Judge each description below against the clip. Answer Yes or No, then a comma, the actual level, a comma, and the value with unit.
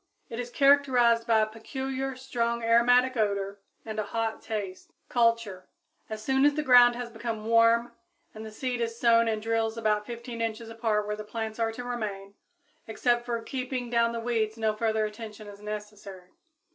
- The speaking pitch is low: No, high, 230 Hz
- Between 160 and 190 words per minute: Yes, average, 175 wpm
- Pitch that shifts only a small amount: Yes, narrow, 2.0 semitones